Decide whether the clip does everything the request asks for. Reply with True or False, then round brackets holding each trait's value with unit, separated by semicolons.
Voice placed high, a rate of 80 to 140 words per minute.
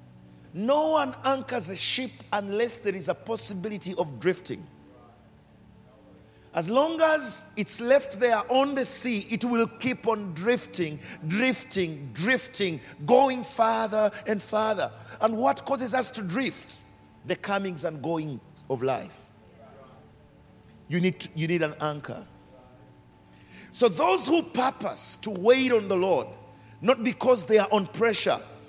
True (215 Hz; 135 wpm)